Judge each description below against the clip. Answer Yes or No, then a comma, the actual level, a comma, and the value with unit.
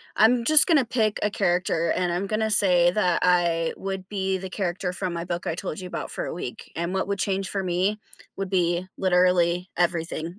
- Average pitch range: No, narrow, 2.1 semitones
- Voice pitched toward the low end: No, medium, 185 Hz